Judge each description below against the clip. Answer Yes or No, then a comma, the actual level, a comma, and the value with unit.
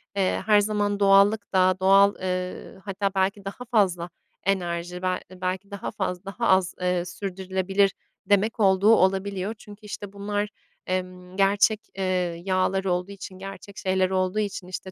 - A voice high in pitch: Yes, high, 195 Hz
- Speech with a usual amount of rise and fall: No, narrow, 1.6 semitones